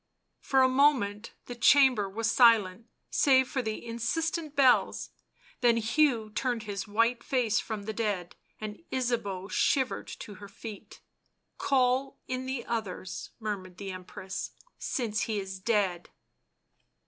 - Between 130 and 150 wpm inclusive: Yes, average, 140 wpm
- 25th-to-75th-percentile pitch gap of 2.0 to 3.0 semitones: No, average, 4.1 semitones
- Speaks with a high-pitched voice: Yes, high, 230 Hz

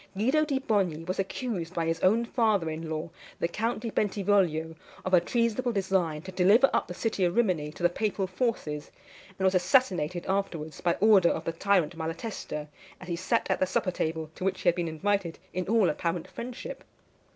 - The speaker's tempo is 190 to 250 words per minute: Yes, average, 195 wpm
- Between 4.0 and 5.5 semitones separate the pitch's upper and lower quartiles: Yes, average, 4.3 semitones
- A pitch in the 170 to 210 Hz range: Yes, medium, 185 Hz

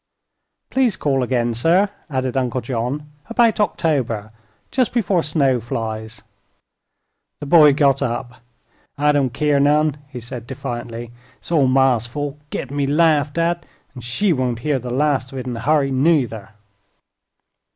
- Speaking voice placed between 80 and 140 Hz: Yes, low, 135 Hz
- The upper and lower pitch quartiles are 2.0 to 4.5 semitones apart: Yes, average, 3.7 semitones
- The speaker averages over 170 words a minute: No, average, 150 wpm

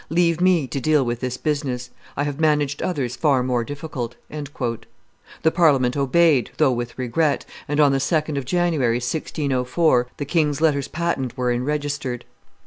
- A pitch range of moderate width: Yes, average, 3.6 semitones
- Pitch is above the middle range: No, medium, 140 Hz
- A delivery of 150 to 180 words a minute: Yes, average, 155 wpm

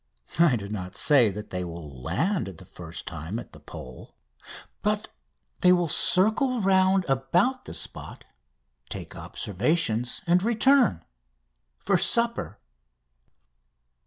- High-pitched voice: No, low, 135 Hz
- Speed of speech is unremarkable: No, slow, 120 wpm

